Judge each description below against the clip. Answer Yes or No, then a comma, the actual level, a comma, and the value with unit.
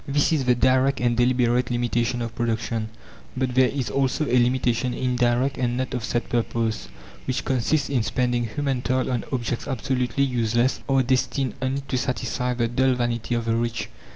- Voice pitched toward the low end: Yes, low, 125 Hz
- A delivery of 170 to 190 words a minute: Yes, average, 180 wpm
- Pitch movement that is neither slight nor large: No, narrow, 1.7 semitones